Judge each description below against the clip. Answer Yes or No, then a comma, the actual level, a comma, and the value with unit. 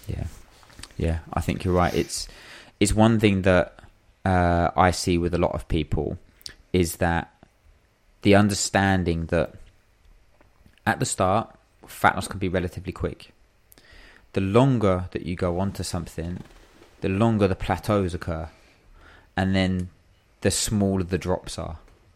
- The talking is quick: No, average, 145 wpm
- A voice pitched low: Yes, very low, 95 Hz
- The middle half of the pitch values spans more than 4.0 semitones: No, narrow, 2.4 semitones